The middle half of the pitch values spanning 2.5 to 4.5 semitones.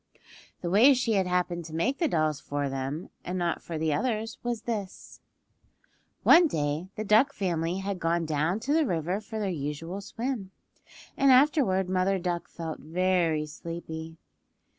No: average, 5.1 semitones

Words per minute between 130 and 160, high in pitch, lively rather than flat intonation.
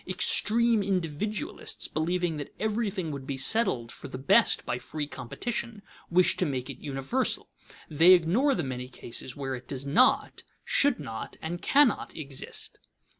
No: average, 150 wpm; medium, 160 Hz; wide, 7.8 semitones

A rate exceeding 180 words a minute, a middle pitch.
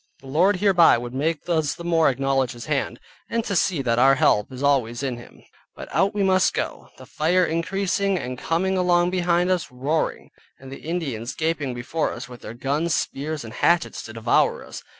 Yes: average, 200 wpm; medium, 155 Hz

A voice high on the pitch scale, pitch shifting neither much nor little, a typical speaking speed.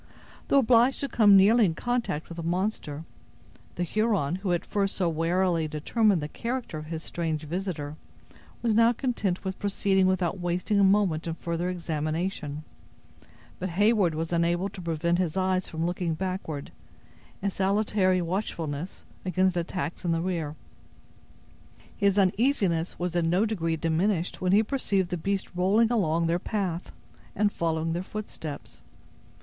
No: medium, 180 Hz; average, 3.4 semitones; average, 155 wpm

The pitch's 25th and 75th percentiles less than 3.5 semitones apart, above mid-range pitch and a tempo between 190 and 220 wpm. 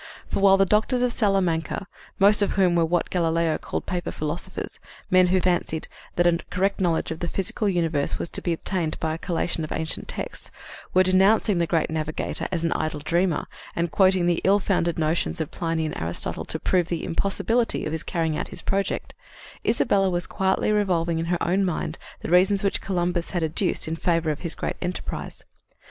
No: average, 2.7 semitones; medium, 175 Hz; average, 195 wpm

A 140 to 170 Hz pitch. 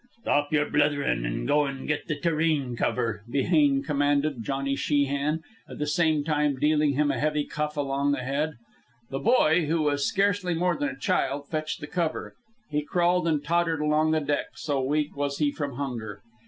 Yes: medium, 150 Hz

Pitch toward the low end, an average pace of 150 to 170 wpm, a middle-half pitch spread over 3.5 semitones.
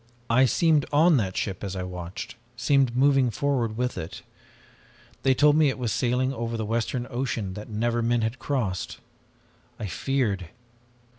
Yes: low, 120 Hz; average, 160 wpm; average, 4.1 semitones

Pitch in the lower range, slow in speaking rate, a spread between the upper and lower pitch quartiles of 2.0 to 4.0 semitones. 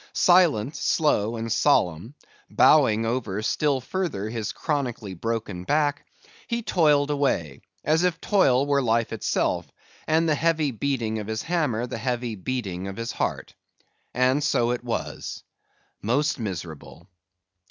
No: low, 125 Hz; slow, 130 wpm; average, 5.2 semitones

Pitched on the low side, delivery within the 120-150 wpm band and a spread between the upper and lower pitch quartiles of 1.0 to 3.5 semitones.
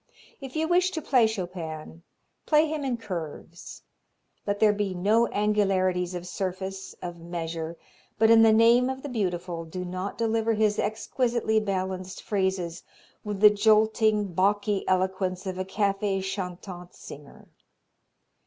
No: high, 195 Hz; average, 140 wpm; average, 3.2 semitones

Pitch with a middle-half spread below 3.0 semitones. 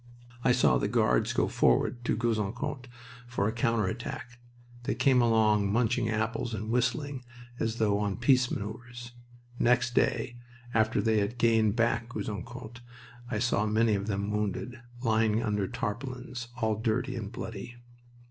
Yes: narrow, 2.4 semitones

